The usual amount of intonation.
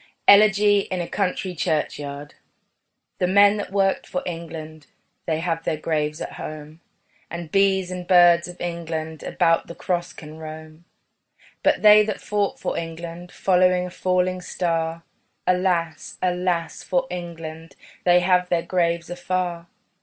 No: narrow, 2.0 semitones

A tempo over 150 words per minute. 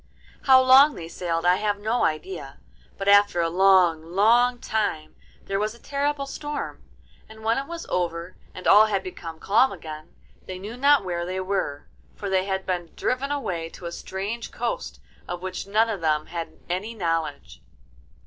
Yes: average, 175 wpm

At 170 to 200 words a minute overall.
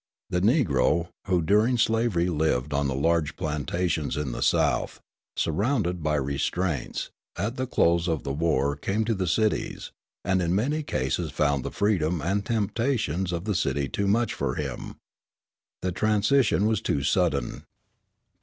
No: average, 155 wpm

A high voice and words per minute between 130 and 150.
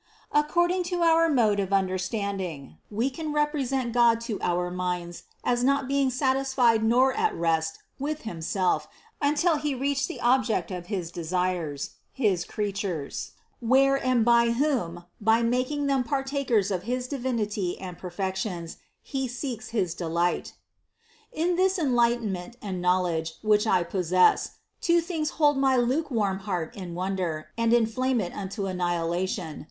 Yes: high, 225 Hz; average, 145 wpm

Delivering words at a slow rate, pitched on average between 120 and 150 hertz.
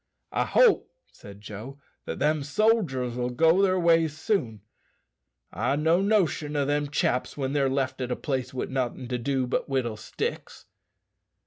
No: average, 155 wpm; medium, 140 Hz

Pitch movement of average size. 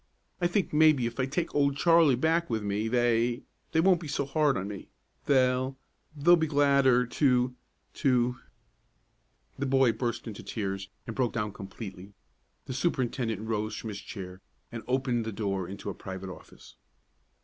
Yes: average, 4.7 semitones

